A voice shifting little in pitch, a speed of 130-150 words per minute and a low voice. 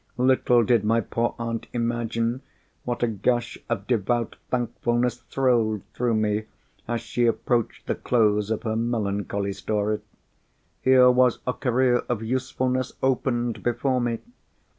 Yes: narrow, 2.1 semitones; slow, 135 wpm; low, 120 Hz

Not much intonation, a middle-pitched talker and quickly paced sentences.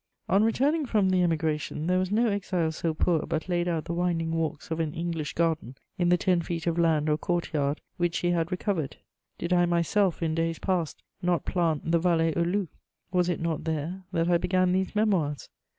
Yes: narrow, 2.0 semitones; medium, 170 Hz; fast, 210 wpm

